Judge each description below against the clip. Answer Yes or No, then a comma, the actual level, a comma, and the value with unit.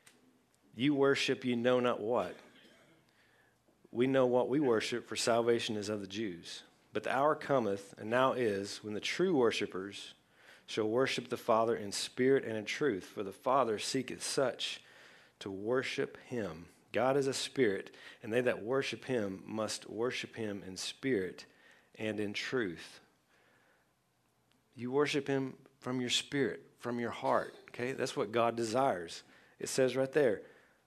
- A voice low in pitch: Yes, low, 120 Hz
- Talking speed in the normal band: Yes, average, 155 wpm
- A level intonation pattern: No, average, 4.0 semitones